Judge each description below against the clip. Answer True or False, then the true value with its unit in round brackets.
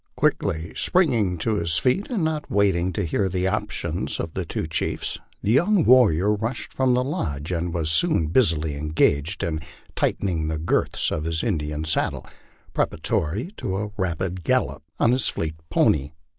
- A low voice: True (90 Hz)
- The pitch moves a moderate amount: False (6.5 semitones)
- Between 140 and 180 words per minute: True (165 wpm)